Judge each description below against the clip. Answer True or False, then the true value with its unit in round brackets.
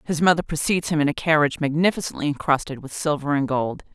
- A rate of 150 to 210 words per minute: True (200 wpm)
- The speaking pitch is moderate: True (150 Hz)